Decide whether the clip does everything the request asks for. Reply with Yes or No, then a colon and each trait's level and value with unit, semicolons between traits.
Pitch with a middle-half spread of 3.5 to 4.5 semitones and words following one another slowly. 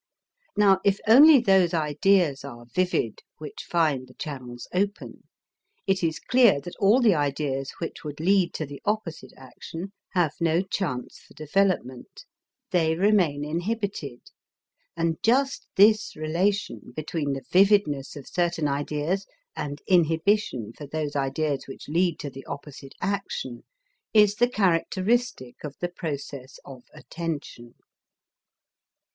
No: wide, 5.5 semitones; slow, 130 wpm